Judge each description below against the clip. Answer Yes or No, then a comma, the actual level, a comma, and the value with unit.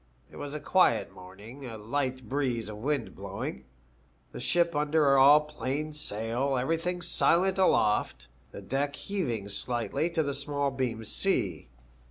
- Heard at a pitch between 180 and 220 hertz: No, medium, 140 Hz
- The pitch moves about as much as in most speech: Yes, average, 4.6 semitones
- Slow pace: No, average, 145 wpm